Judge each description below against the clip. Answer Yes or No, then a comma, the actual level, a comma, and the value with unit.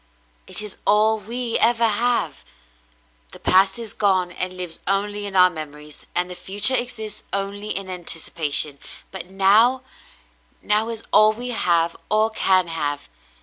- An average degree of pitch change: Yes, average, 3.4 semitones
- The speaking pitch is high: Yes, high, 195 Hz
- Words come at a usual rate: Yes, average, 150 wpm